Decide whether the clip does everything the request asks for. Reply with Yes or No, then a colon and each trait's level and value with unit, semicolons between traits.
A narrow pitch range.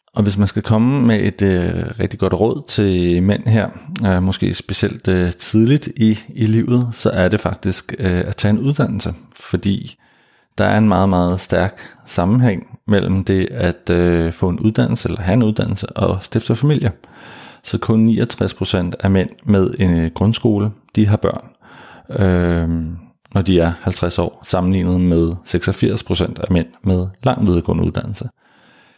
No: average, 3.4 semitones